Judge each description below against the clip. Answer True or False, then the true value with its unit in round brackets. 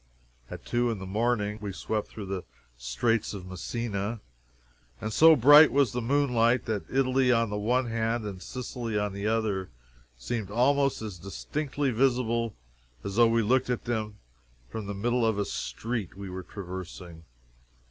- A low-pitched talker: True (115 Hz)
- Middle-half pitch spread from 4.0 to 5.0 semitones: False (3.5 semitones)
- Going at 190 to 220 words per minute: False (165 wpm)